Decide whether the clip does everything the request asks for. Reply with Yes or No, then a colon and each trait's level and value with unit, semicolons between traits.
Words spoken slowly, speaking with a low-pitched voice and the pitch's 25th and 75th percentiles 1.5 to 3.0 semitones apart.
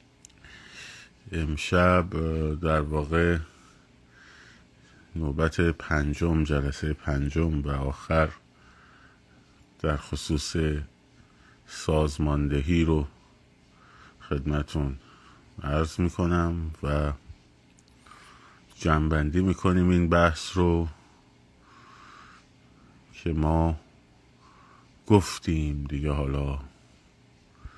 Yes: slow, 60 wpm; very low, 75 Hz; narrow, 2.6 semitones